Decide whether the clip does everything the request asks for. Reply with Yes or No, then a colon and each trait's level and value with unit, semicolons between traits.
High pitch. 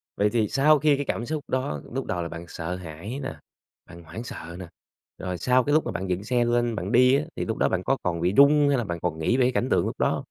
No: low, 115 Hz